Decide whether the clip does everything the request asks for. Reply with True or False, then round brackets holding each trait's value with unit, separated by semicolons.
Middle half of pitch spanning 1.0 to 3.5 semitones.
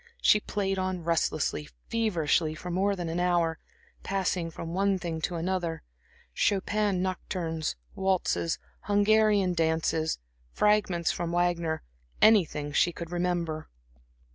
True (2.8 semitones)